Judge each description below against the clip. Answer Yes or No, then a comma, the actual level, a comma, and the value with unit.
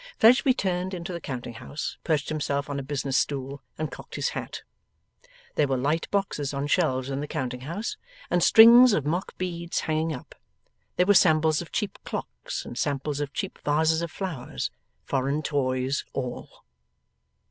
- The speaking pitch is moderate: Yes, medium, 150 Hz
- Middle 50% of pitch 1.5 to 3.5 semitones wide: No, average, 4.2 semitones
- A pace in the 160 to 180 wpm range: Yes, average, 170 wpm